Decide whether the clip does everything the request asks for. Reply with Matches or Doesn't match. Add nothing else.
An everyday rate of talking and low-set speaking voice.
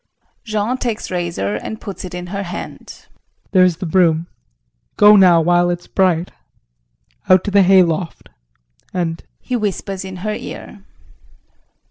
Doesn't match